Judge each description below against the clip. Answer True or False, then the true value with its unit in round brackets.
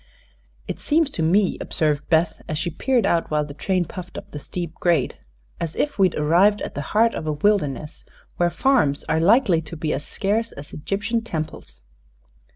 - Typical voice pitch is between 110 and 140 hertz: False (170 Hz)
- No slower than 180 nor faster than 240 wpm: True (185 wpm)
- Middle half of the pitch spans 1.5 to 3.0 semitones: False (5.2 semitones)